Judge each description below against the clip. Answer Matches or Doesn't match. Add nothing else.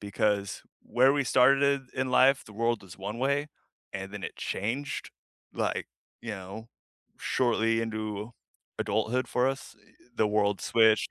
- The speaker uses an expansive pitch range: Doesn't match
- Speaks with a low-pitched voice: Matches